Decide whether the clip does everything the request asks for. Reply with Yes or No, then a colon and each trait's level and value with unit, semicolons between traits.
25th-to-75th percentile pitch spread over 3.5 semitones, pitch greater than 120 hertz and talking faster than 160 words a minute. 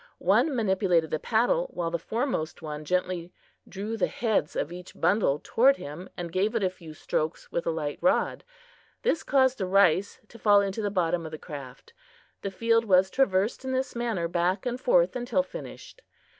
Yes: wide, 5.6 semitones; high, 190 Hz; average, 185 wpm